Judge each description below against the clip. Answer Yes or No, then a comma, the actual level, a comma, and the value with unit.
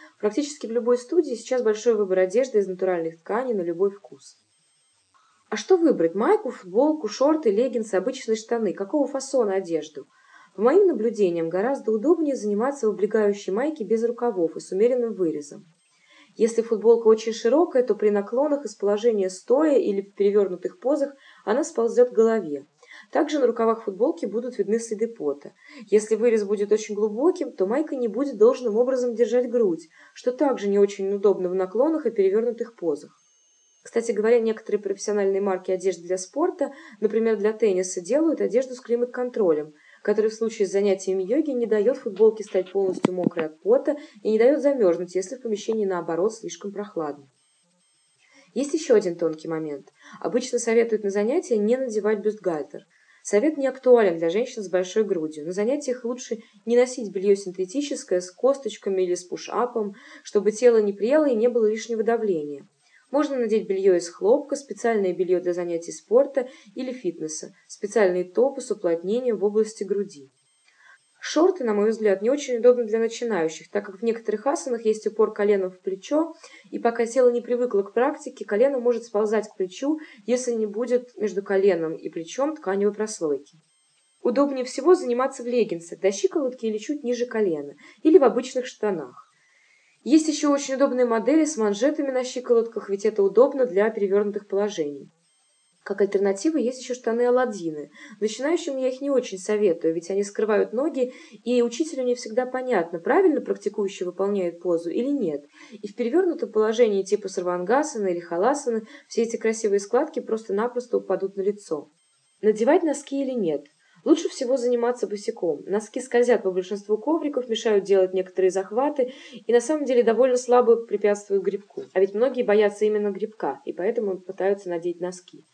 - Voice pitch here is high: Yes, high, 225 Hz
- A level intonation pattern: No, average, 4.3 semitones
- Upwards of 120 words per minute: Yes, fast, 160 wpm